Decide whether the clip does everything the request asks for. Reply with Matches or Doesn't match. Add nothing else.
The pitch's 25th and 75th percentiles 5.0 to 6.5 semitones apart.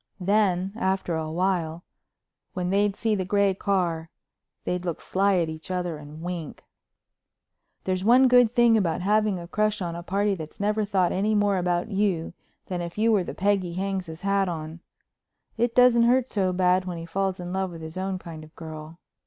Doesn't match